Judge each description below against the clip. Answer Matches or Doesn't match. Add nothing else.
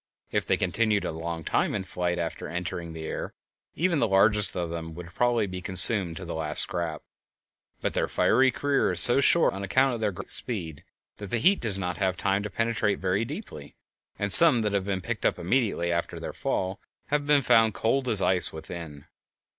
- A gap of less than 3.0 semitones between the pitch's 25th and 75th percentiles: Doesn't match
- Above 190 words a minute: Matches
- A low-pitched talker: Matches